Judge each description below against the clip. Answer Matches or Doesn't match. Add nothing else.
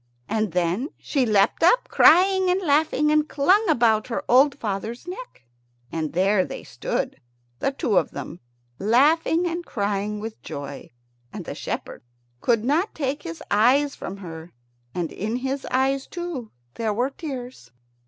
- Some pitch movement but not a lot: Doesn't match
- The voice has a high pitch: Matches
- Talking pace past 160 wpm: Doesn't match